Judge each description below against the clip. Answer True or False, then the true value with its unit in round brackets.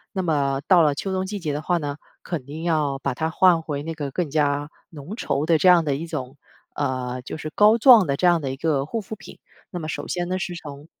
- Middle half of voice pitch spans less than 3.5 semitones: False (3.8 semitones)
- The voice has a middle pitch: True (155 Hz)